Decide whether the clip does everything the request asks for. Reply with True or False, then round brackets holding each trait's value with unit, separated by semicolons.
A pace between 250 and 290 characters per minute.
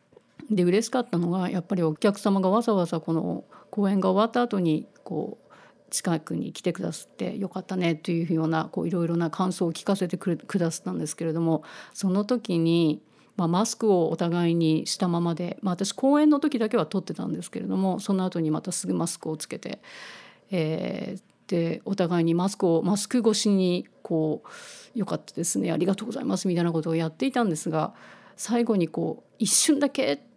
False (390 characters per minute)